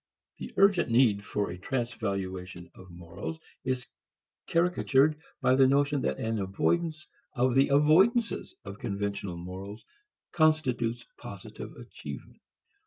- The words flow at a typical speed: No, slow, 115 wpm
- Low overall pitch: Yes, low, 125 Hz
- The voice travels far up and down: Yes, wide, 7.4 semitones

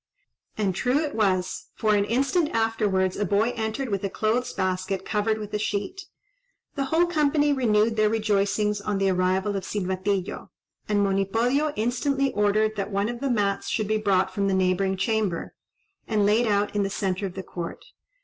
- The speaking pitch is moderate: No, high, 210 Hz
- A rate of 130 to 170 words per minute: No, average, 180 wpm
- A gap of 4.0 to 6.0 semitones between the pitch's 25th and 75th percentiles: No, narrow, 2.6 semitones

